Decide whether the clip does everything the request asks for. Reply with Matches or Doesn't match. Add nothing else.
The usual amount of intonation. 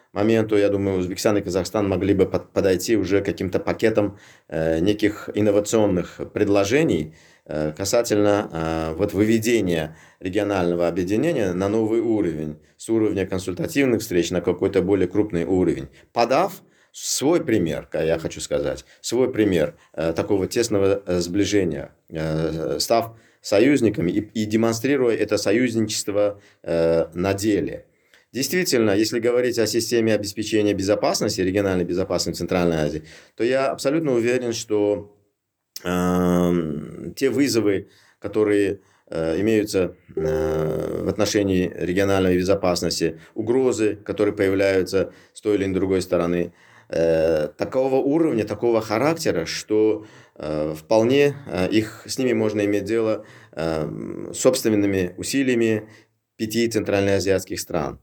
Matches